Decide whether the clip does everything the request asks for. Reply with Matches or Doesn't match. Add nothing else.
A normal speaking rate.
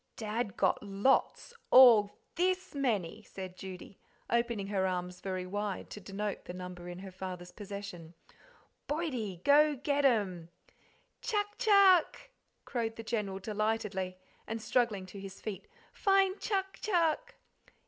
Doesn't match